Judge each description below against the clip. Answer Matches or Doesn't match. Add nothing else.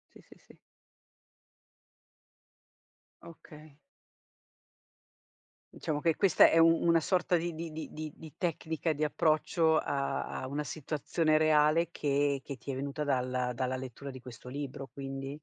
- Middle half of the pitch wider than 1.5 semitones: Matches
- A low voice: Doesn't match